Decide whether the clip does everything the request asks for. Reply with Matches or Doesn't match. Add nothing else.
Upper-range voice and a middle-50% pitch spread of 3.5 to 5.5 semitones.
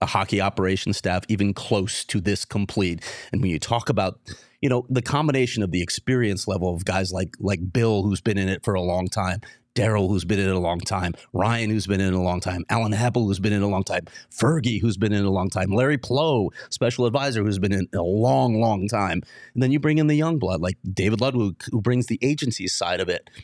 Doesn't match